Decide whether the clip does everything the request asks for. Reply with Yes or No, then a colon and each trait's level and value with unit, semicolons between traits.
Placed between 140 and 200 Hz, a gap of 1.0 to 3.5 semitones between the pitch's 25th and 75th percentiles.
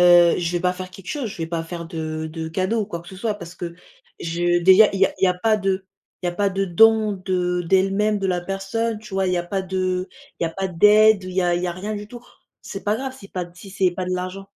Yes: medium, 185 Hz; narrow, 2.5 semitones